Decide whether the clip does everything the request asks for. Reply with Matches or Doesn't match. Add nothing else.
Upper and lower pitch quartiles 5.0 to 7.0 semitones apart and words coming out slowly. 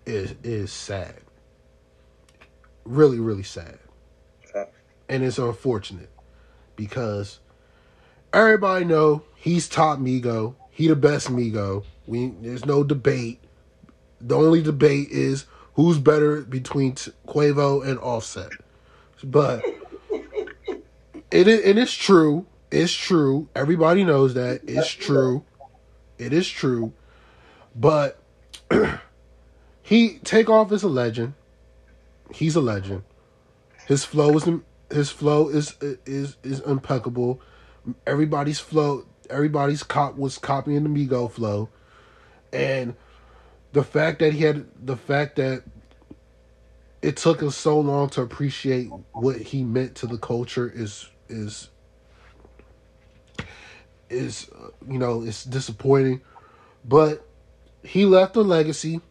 Matches